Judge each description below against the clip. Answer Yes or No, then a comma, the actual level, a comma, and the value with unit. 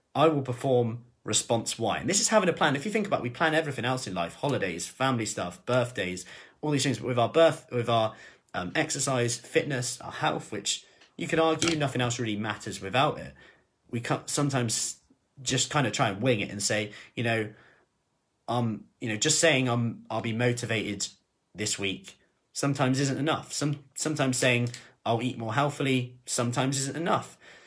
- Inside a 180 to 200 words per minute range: Yes, average, 190 wpm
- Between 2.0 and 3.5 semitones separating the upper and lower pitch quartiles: No, average, 3.9 semitones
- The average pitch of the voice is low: Yes, low, 125 Hz